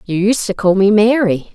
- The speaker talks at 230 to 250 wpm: Yes, fast, 235 wpm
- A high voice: Yes, high, 205 Hz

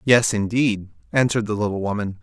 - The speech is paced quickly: No, average, 160 wpm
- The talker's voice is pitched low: Yes, low, 110 Hz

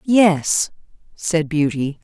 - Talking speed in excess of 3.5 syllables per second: No, 2.7 syllables/s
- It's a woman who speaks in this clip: Yes, female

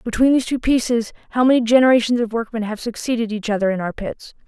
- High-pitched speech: Yes, high, 230 Hz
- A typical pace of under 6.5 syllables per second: No, 6.6 syllables/s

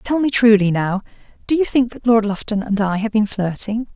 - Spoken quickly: Yes, fast, 230 wpm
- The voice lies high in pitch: Yes, high, 220 Hz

